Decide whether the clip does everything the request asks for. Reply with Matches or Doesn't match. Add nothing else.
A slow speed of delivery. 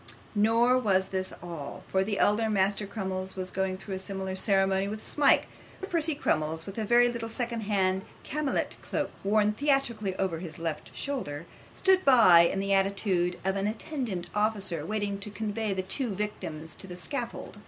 Doesn't match